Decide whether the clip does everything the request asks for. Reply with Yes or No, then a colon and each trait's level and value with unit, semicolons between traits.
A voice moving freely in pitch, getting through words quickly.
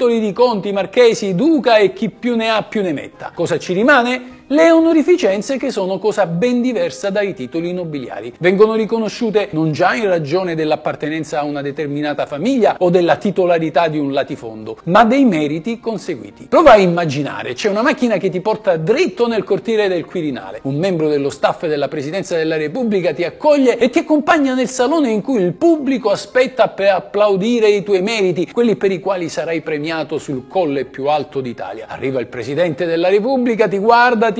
Yes: wide, 6.5 semitones; fast, 180 wpm